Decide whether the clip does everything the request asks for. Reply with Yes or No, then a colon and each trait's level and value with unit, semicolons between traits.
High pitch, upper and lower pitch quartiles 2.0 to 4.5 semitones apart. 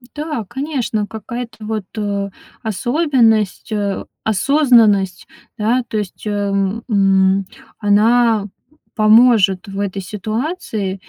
Yes: high, 215 Hz; average, 3.2 semitones